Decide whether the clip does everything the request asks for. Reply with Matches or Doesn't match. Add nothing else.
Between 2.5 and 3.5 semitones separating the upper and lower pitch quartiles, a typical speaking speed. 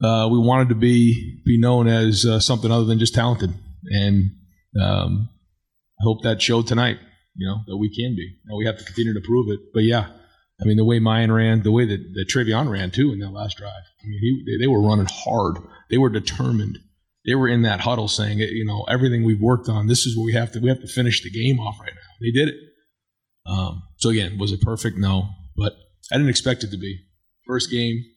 Doesn't match